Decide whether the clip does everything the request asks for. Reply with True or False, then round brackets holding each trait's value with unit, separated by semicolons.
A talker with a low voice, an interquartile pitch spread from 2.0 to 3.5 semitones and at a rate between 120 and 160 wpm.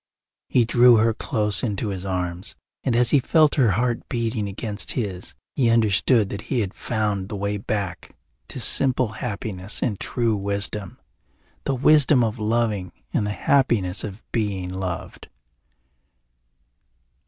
True (105 Hz; 3.2 semitones; 140 wpm)